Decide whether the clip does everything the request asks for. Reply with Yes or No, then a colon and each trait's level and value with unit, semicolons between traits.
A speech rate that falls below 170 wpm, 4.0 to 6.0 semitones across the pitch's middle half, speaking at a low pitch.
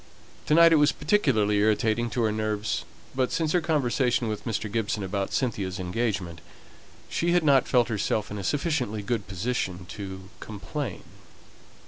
Yes: average, 155 wpm; average, 4.6 semitones; low, 110 Hz